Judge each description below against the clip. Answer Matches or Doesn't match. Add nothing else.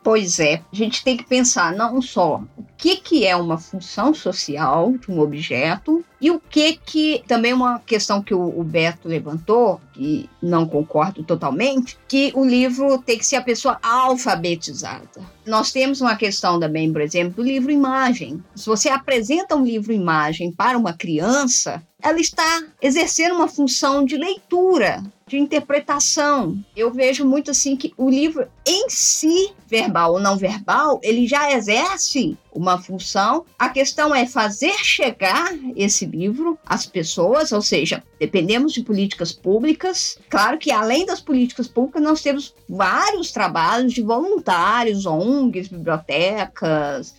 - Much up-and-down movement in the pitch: Matches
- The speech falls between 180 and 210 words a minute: Doesn't match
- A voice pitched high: Matches